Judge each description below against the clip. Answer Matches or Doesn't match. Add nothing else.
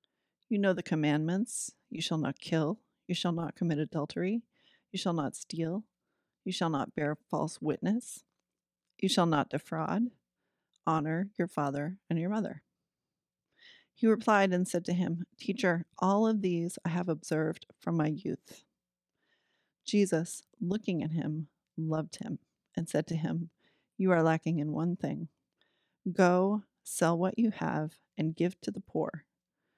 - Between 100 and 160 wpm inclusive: Matches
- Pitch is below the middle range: Doesn't match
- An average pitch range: Matches